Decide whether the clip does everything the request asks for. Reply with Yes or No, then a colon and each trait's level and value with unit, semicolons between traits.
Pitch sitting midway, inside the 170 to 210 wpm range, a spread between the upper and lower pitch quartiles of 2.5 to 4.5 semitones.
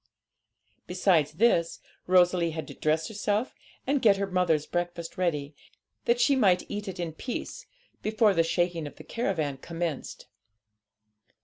No: medium, 180 Hz; average, 140 wpm; average, 3.8 semitones